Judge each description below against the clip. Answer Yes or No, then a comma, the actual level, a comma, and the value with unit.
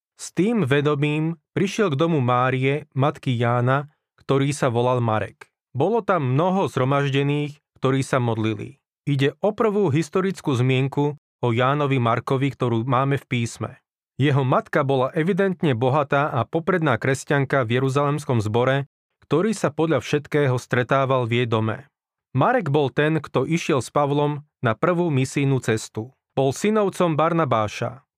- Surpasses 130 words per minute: Yes, average, 140 wpm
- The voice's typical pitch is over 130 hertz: Yes, medium, 140 Hz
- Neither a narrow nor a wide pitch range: Yes, average, 3.3 semitones